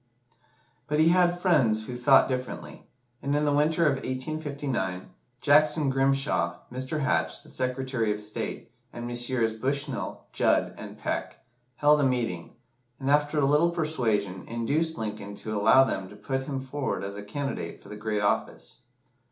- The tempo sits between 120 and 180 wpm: Yes, average, 160 wpm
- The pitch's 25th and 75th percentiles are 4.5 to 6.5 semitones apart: Yes, average, 5.0 semitones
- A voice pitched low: Yes, low, 130 Hz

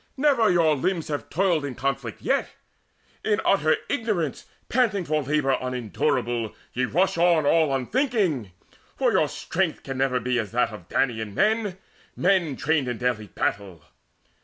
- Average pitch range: No, wide, 6.8 semitones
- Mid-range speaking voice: Yes, medium, 145 Hz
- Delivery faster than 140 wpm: Yes, average, 150 wpm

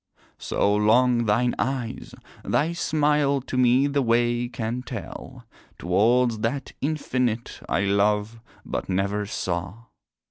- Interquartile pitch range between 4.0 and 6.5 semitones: No, average, 3.5 semitones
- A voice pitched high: No, low, 120 Hz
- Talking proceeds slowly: Yes, slow, 115 wpm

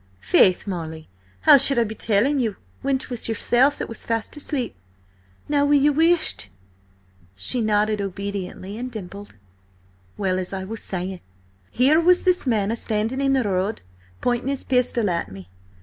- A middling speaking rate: Yes, average, 155 wpm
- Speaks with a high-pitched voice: Yes, high, 225 Hz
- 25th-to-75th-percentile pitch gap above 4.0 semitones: Yes, wide, 5.6 semitones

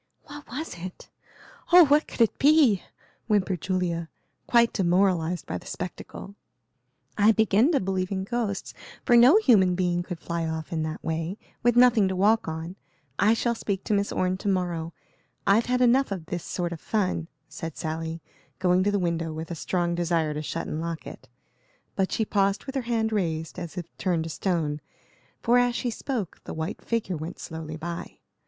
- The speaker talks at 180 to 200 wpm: Yes, average, 190 wpm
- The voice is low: No, medium, 185 Hz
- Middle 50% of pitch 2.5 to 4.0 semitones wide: No, average, 4.9 semitones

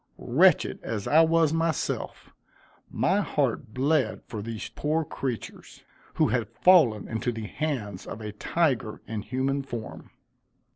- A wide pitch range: Yes, wide, 6.1 semitones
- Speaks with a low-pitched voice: Yes, low, 130 Hz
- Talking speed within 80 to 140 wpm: Yes, slow, 135 wpm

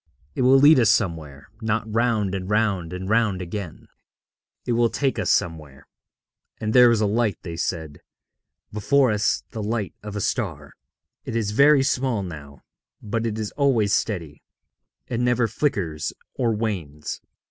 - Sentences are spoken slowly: No, average, 160 wpm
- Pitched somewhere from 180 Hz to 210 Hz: No, low, 105 Hz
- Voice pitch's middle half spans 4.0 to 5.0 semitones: Yes, average, 4.5 semitones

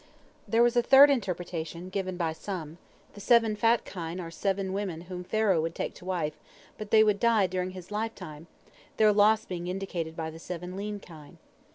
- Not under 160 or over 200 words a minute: Yes, average, 190 wpm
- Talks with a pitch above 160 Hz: Yes, medium, 185 Hz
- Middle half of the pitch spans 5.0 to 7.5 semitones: No, average, 3.8 semitones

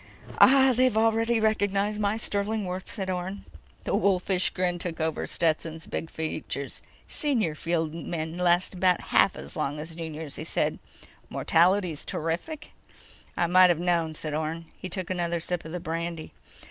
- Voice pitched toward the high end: No, medium, 175 Hz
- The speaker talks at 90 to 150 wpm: No, average, 160 wpm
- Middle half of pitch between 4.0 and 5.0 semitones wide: No, average, 3.6 semitones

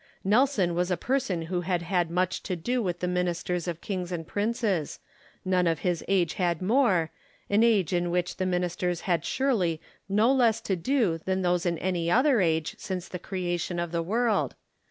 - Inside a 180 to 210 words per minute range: Yes, average, 195 wpm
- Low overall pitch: No, medium, 180 Hz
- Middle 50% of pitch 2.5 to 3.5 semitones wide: Yes, average, 2.8 semitones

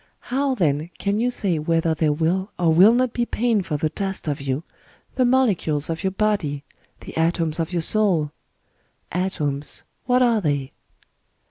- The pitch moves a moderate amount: No, wide, 5.7 semitones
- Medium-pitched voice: Yes, medium, 175 Hz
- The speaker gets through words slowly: No, average, 175 wpm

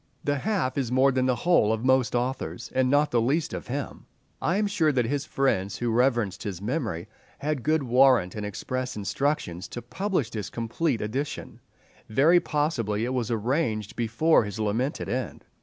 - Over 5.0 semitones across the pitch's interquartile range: No, average, 4.6 semitones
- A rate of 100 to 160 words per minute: No, average, 175 wpm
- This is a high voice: No, low, 125 Hz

